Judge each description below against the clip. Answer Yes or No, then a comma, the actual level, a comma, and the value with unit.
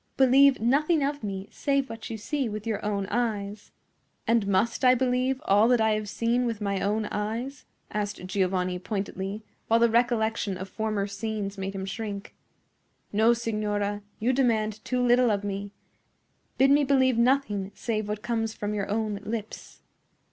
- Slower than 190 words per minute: Yes, average, 165 wpm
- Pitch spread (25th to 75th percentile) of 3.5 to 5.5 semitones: No, average, 3.1 semitones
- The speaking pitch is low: No, high, 220 Hz